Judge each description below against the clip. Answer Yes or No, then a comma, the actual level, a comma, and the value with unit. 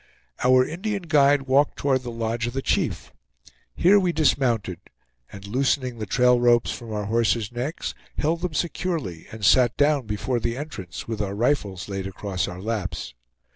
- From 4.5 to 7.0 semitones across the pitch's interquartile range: Yes, wide, 5.5 semitones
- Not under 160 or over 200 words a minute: Yes, average, 170 wpm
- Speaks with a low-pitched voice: Yes, low, 120 Hz